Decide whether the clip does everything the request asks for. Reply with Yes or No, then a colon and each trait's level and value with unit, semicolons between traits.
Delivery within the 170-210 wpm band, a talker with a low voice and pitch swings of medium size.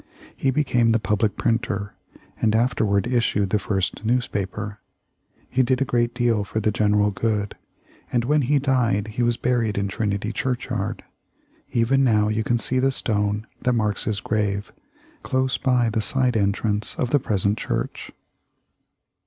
No: average, 160 wpm; low, 110 Hz; average, 3.2 semitones